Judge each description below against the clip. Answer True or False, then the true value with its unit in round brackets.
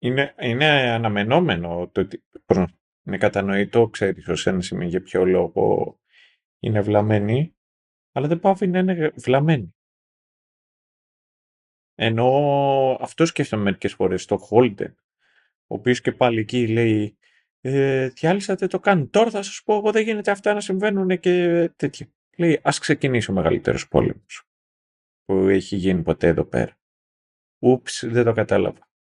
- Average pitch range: False (8.3 semitones)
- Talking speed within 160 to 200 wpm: False (140 wpm)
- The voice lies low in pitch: True (125 Hz)